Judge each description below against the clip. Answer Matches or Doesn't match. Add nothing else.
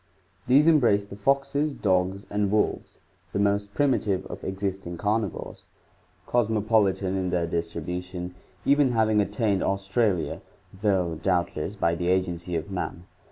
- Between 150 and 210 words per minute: Doesn't match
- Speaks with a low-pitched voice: Matches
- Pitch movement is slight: Doesn't match